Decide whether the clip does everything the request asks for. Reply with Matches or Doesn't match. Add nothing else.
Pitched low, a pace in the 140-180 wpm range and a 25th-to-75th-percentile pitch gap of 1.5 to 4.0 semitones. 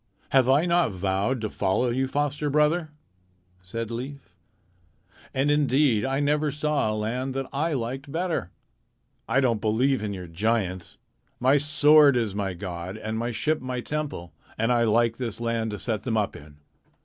Doesn't match